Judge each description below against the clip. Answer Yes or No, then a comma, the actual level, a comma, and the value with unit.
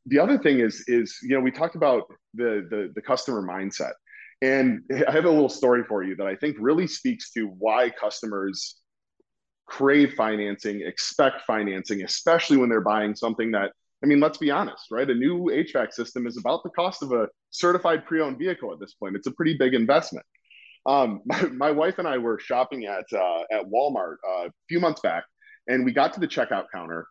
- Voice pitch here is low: Yes, low, 130 Hz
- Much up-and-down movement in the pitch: Yes, wide, 6.6 semitones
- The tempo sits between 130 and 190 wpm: No, fast, 205 wpm